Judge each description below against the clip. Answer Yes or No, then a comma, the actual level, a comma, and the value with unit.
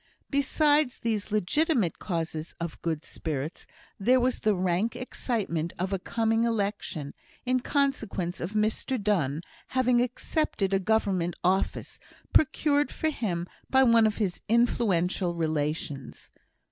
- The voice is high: Yes, high, 205 Hz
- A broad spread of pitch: Yes, wide, 6.1 semitones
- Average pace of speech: No, slow, 125 wpm